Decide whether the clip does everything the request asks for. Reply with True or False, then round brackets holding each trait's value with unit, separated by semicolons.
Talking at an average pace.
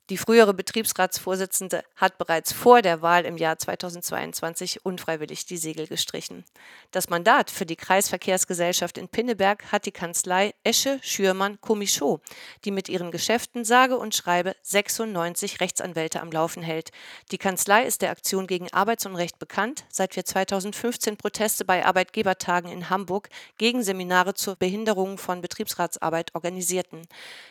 True (135 wpm)